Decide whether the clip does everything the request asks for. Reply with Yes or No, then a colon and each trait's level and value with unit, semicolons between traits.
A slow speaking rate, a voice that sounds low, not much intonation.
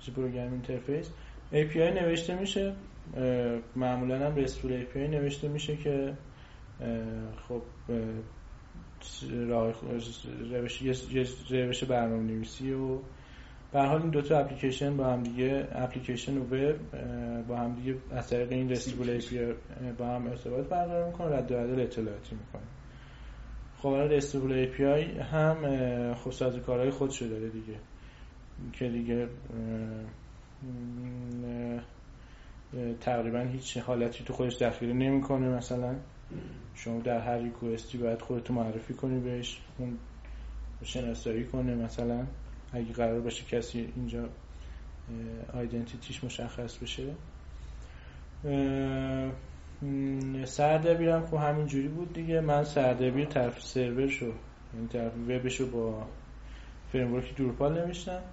No: average, 115 wpm; low, 125 Hz; narrow, 2.3 semitones